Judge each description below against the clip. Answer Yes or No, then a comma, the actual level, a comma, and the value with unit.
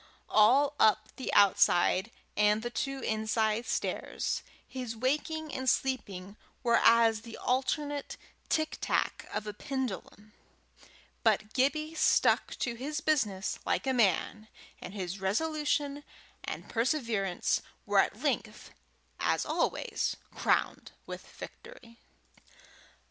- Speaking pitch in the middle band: No, high, 235 Hz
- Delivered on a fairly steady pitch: No, average, 4.8 semitones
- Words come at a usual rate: No, slow, 110 wpm